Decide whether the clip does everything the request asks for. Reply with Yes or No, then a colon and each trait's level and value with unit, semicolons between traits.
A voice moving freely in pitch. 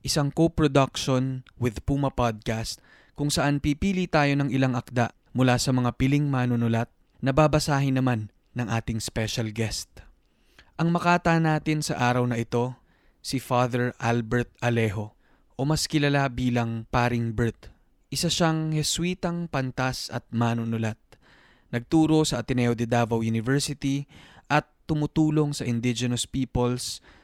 No: average, 3.7 semitones